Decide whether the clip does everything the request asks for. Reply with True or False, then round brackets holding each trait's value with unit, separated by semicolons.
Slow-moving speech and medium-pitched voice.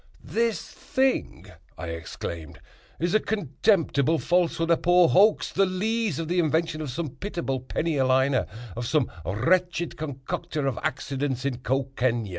True (130 wpm; 155 Hz)